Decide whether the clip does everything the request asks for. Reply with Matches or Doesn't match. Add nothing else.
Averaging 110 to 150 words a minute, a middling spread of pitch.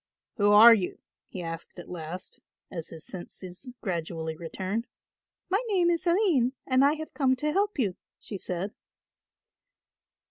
Doesn't match